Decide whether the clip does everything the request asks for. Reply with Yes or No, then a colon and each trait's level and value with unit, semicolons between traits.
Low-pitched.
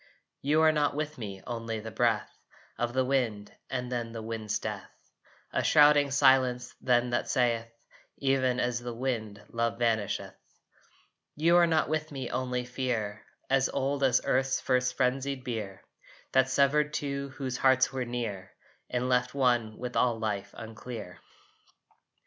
Yes: low, 125 Hz